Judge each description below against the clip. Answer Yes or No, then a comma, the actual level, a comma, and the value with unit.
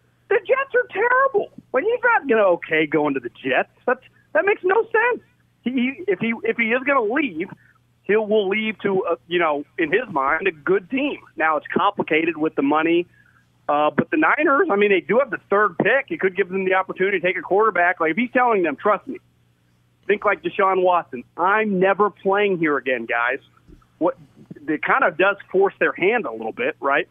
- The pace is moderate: No, fast, 210 wpm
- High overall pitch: Yes, high, 200 Hz